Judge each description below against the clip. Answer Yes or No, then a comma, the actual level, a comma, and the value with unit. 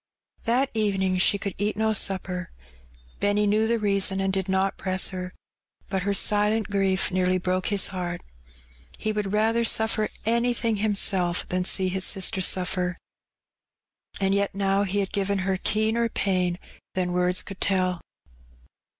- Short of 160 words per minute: Yes, average, 150 wpm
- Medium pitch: No, high, 195 Hz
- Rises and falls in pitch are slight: Yes, narrow, 2.2 semitones